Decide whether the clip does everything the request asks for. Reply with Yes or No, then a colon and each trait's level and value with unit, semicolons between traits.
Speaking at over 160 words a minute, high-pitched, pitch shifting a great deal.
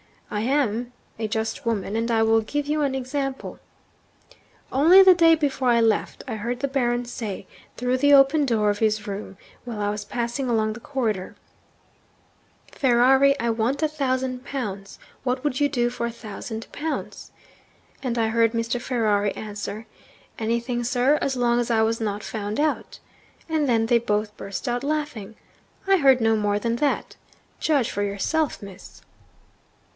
No: average, 170 wpm; high, 240 Hz; average, 3.7 semitones